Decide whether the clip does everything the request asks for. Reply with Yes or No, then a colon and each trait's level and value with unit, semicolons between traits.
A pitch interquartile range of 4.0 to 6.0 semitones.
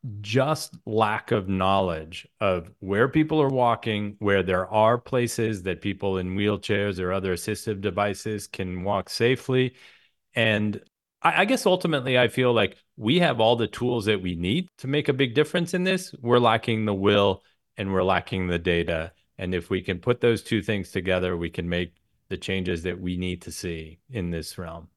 Yes: average, 4.6 semitones